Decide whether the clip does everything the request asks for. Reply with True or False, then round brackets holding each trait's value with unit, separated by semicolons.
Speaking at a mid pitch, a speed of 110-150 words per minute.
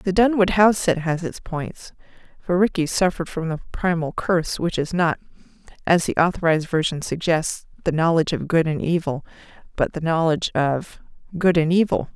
False (170 Hz; 165 wpm)